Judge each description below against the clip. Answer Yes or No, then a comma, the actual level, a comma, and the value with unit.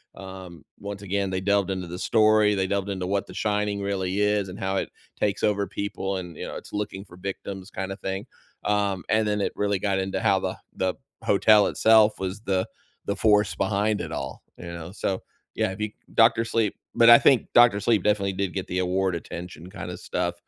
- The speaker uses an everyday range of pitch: No, narrow, 1.8 semitones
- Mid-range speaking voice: No, low, 100 Hz